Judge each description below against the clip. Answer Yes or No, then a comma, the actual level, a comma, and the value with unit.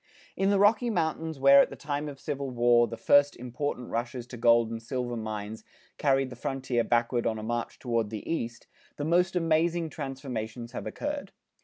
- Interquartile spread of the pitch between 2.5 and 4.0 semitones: No, average, 4.5 semitones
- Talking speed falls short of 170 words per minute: No, average, 185 wpm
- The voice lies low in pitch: Yes, low, 130 Hz